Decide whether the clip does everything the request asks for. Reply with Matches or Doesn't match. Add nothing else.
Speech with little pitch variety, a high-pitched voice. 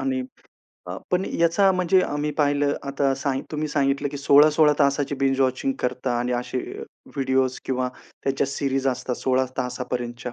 Doesn't match